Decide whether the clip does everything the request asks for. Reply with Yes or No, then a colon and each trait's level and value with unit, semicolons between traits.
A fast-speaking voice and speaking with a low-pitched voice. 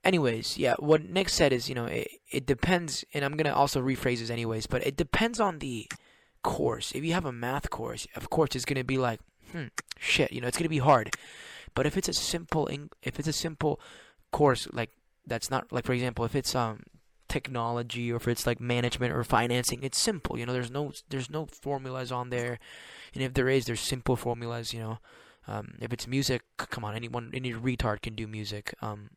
Yes: fast, 215 wpm; low, 125 Hz